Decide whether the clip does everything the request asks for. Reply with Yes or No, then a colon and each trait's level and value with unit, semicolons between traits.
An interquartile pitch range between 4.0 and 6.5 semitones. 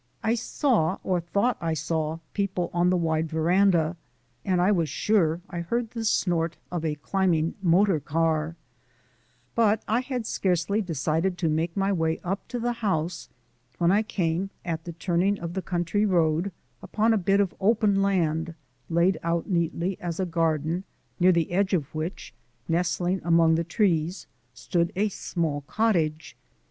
No: average, 3.3 semitones